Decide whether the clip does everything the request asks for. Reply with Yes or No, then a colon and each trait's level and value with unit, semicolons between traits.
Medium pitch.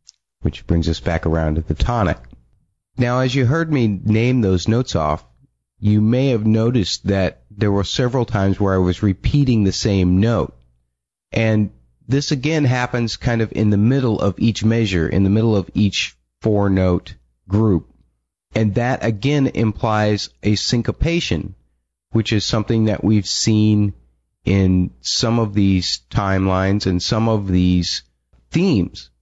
No: low, 105 Hz